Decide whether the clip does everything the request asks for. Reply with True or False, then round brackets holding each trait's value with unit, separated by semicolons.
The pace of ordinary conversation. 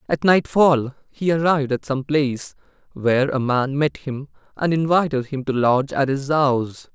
True (175 wpm)